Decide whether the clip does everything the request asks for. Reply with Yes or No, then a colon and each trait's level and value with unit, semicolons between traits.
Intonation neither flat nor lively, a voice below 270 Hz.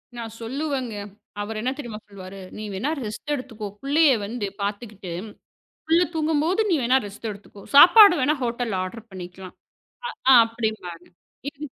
No: wide, 5.9 semitones; high, 230 Hz